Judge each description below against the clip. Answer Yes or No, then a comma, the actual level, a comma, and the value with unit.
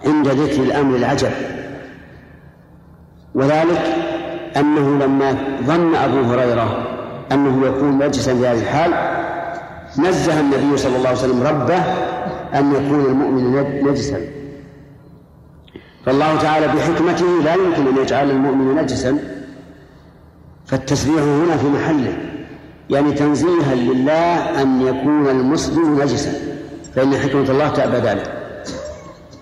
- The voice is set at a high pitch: No, medium, 140 Hz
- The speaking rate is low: No, average, 105 wpm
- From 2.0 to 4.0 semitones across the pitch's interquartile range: Yes, narrow, 2.6 semitones